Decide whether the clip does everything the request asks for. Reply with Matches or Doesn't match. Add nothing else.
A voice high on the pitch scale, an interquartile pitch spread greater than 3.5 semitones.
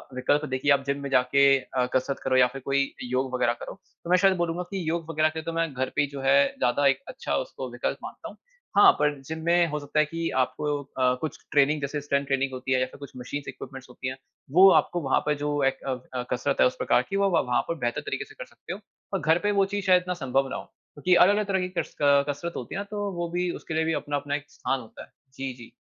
Doesn't match